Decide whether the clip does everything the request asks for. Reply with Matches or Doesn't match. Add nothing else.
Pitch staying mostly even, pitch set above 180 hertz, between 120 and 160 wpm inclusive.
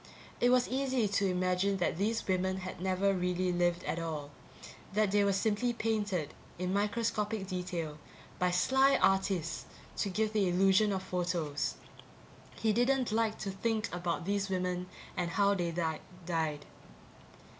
Doesn't match